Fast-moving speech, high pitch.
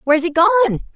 No: average, 190 wpm; very high, 335 Hz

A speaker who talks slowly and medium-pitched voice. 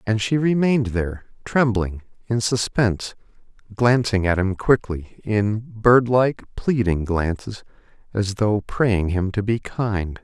No: slow, 130 wpm; low, 110 Hz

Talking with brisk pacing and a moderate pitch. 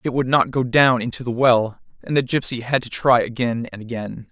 No: fast, 235 wpm; low, 125 Hz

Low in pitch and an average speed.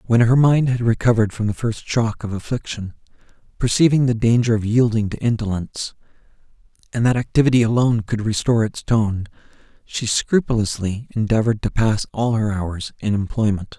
Yes: low, 115 Hz; average, 155 wpm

